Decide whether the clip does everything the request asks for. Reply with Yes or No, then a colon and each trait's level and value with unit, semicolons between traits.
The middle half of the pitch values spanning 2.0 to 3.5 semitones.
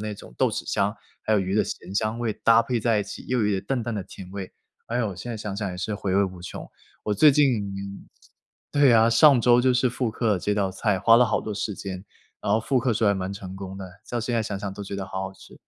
Yes: average, 3.2 semitones